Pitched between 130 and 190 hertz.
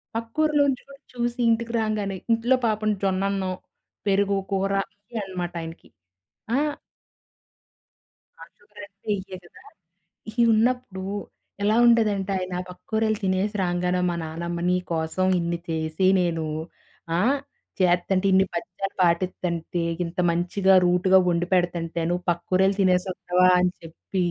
Yes: medium, 185 Hz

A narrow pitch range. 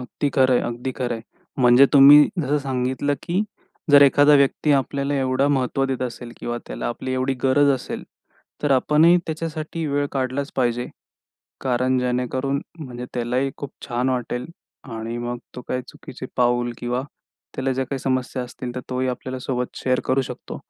Yes: narrow, 2.0 semitones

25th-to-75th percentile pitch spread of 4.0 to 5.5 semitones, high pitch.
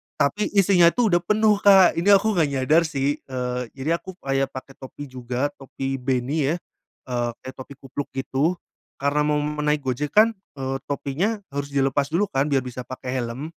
No: average, 4.3 semitones; medium, 140 Hz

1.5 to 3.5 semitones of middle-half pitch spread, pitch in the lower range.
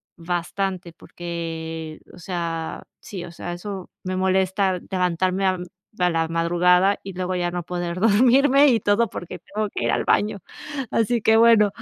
No: average, 2.7 semitones; medium, 185 Hz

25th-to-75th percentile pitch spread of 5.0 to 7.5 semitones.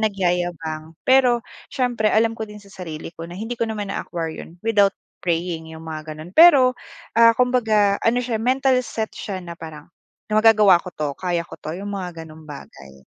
Yes: wide, 5.6 semitones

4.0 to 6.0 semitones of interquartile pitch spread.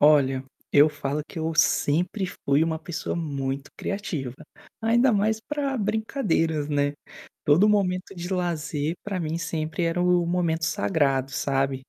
Yes: average, 4.5 semitones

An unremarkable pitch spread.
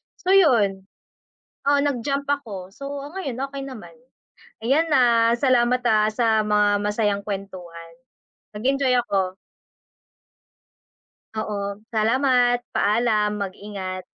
Yes: average, 4.2 semitones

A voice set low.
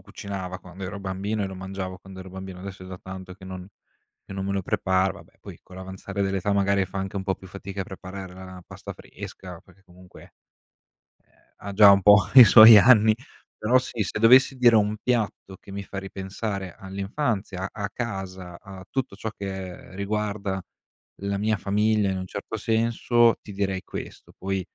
Yes: very low, 95 Hz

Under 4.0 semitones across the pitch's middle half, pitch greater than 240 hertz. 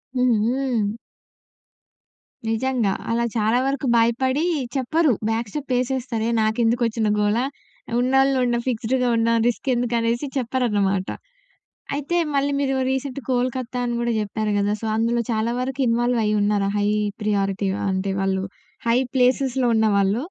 No: average, 3.1 semitones; high, 235 Hz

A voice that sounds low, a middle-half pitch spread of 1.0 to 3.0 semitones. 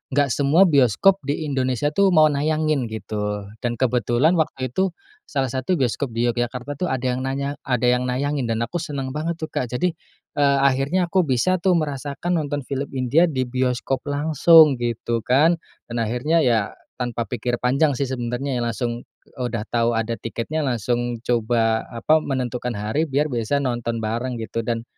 No: low, 130 Hz; average, 3.6 semitones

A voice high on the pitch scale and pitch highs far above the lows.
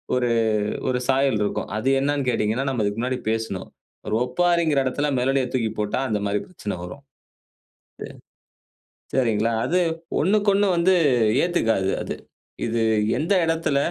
No: low, 130 Hz; wide, 6.5 semitones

